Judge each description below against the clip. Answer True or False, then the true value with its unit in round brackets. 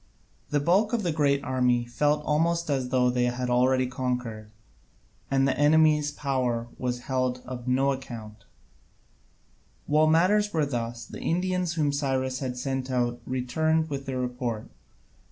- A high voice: False (130 Hz)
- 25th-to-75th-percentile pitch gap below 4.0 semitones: True (3.4 semitones)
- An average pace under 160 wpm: True (150 wpm)